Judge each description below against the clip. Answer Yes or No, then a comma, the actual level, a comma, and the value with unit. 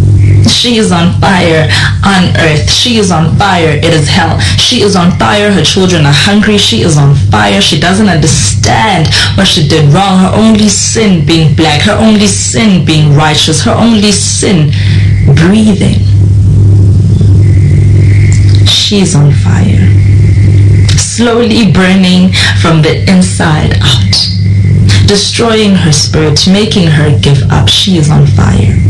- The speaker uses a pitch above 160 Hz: No, low, 125 Hz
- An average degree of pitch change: No, wide, 8.6 semitones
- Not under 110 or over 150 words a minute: Yes, average, 140 wpm